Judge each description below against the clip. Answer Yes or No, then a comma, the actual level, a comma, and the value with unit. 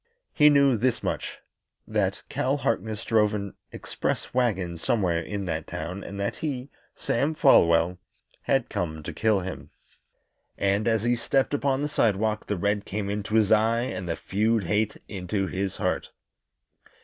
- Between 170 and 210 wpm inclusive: No, average, 160 wpm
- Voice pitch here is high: No, low, 105 Hz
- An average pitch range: Yes, average, 3.8 semitones